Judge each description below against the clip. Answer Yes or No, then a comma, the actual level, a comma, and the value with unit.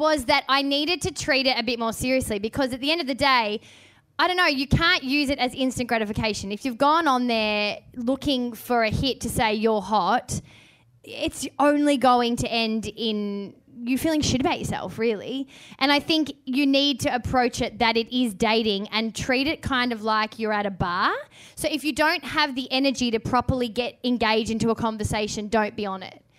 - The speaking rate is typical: No, fast, 210 wpm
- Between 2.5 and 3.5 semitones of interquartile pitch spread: No, average, 4.1 semitones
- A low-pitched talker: No, high, 245 Hz